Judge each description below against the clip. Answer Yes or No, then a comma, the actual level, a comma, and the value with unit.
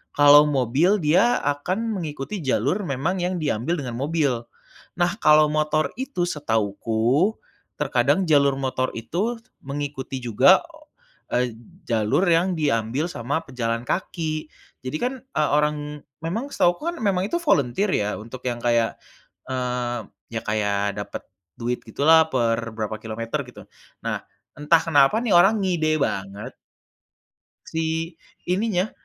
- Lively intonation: Yes, wide, 5.9 semitones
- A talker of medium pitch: Yes, medium, 145 Hz